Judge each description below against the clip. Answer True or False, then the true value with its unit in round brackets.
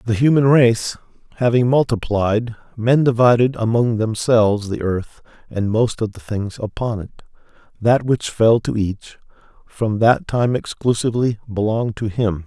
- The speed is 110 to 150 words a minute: True (145 wpm)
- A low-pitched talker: True (115 Hz)